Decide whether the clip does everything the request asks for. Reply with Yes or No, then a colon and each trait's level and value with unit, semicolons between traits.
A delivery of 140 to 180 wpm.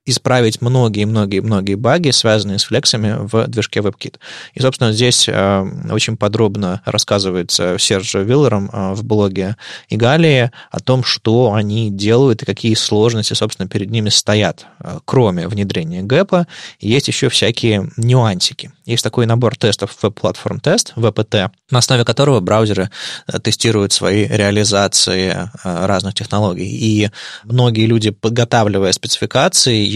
No: average, 130 wpm